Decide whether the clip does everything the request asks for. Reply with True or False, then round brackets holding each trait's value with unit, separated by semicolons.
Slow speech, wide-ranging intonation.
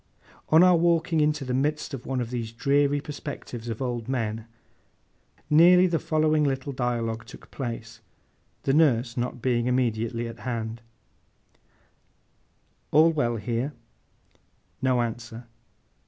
False (125 wpm; 4.3 semitones)